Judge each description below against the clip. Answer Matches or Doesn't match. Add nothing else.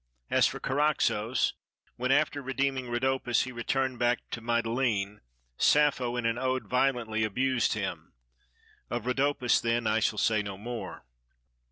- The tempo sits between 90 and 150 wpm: Matches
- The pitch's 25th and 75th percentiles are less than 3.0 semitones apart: Matches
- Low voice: Matches